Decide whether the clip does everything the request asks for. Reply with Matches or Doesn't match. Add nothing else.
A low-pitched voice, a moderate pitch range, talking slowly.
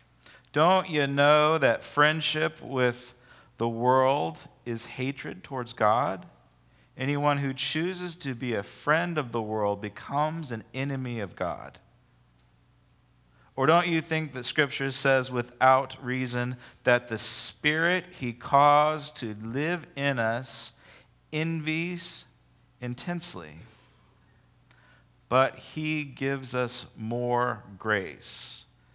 Matches